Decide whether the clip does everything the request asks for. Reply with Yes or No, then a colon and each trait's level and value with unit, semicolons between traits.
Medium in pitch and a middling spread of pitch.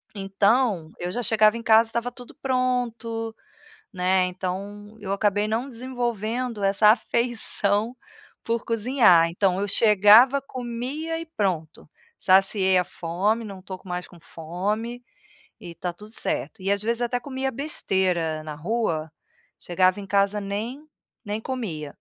No: high, 210 Hz; average, 4.0 semitones